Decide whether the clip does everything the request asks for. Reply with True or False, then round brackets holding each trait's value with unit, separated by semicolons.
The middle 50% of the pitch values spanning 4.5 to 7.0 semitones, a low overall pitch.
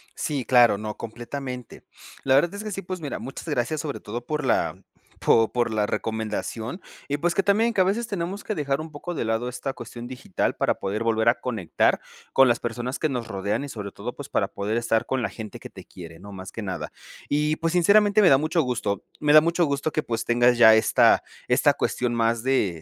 True (5.6 semitones; 125 Hz)